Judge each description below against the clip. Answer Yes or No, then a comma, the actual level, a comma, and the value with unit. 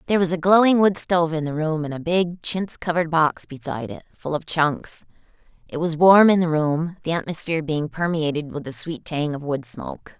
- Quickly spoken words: Yes, fast, 220 wpm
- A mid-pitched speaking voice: Yes, medium, 160 Hz